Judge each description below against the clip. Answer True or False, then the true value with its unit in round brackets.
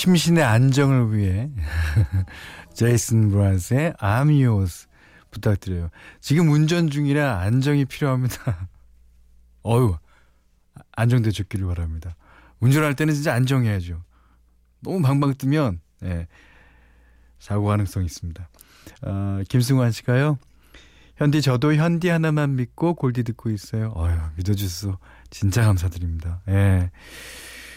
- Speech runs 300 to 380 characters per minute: False (260 characters per minute)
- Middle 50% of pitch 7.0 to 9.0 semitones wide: True (7.5 semitones)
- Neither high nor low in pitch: False (100 Hz)